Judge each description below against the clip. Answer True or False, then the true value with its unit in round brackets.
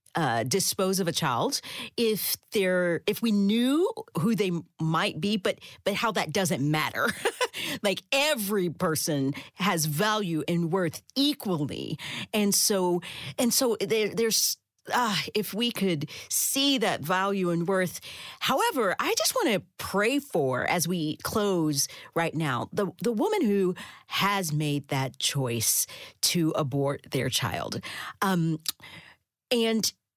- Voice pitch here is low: False (185 Hz)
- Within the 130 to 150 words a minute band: True (135 wpm)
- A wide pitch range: True (5.7 semitones)